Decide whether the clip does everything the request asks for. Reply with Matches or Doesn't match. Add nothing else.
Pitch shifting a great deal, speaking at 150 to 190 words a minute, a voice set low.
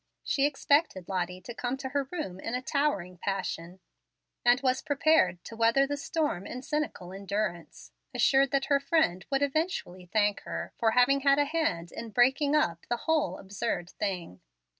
Doesn't match